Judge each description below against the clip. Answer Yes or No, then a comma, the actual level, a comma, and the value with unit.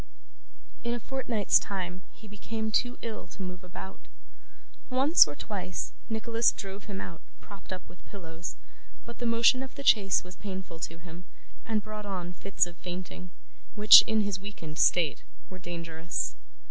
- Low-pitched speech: No, high, 195 Hz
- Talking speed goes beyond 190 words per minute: No, average, 160 wpm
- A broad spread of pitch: No, average, 3.7 semitones